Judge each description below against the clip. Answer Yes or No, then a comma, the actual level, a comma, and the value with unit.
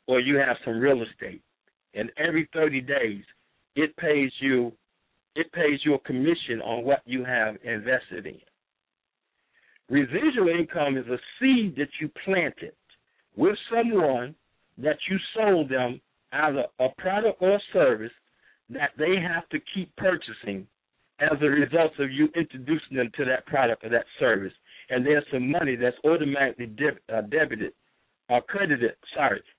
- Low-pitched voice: No, medium, 145 Hz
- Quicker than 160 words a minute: No, average, 150 wpm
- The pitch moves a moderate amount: Yes, average, 4.7 semitones